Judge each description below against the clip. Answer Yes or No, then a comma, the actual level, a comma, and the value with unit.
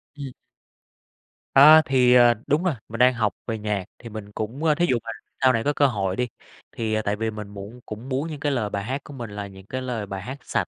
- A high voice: No, low, 120 Hz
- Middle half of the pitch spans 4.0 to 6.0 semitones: Yes, average, 4.3 semitones